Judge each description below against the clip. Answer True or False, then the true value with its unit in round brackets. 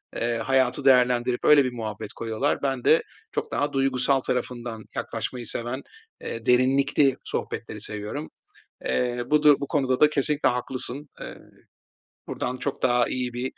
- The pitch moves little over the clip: True (2.3 semitones)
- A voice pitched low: True (125 Hz)